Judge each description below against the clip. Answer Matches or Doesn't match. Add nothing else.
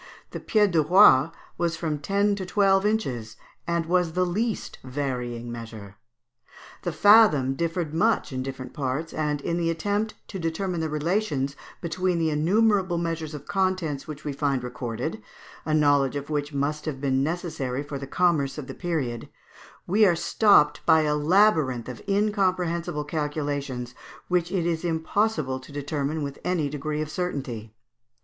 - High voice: Doesn't match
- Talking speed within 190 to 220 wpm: Doesn't match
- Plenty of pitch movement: Doesn't match